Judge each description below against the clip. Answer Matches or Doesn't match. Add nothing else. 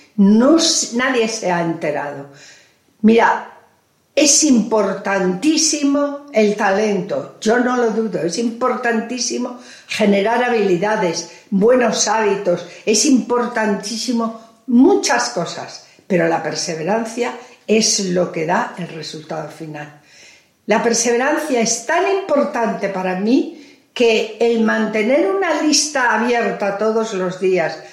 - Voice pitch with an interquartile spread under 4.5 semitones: Doesn't match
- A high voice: Matches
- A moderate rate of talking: Doesn't match